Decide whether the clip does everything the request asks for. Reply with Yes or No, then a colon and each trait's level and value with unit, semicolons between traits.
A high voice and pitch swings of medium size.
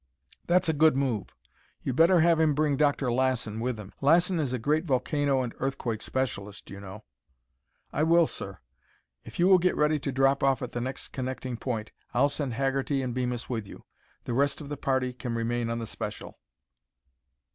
No: low, 130 Hz; average, 3.6 semitones